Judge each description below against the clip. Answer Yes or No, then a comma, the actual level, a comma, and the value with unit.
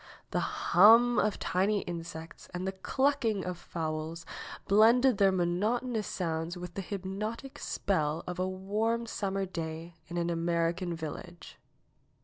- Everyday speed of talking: No, slow, 130 wpm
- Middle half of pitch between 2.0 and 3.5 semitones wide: No, average, 3.9 semitones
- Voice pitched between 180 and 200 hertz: Yes, medium, 185 Hz